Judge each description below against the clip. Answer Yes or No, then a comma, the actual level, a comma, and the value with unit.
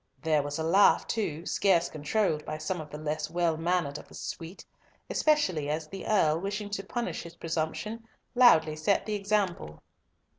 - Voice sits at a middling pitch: Yes, medium, 170 Hz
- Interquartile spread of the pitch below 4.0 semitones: No, average, 4.5 semitones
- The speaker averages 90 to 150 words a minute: No, average, 175 wpm